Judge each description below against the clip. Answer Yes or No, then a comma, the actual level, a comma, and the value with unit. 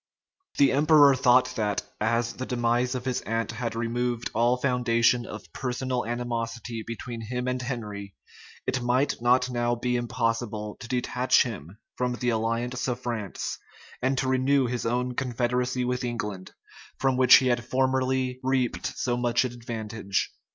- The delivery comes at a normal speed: Yes, average, 155 wpm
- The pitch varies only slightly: Yes, narrow, 1.6 semitones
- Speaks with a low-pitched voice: Yes, low, 120 Hz